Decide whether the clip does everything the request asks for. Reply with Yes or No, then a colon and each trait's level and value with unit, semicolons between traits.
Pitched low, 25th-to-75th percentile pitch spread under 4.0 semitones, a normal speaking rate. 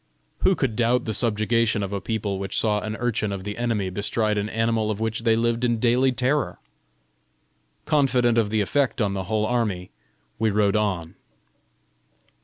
Yes: low, 110 Hz; narrow, 2.4 semitones; average, 175 wpm